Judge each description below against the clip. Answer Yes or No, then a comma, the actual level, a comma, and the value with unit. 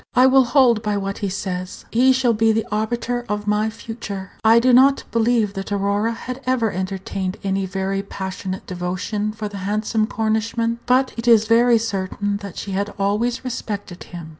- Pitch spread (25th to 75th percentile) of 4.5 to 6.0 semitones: No, average, 3.0 semitones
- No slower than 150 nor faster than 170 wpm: No, average, 180 wpm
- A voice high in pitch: Yes, high, 215 Hz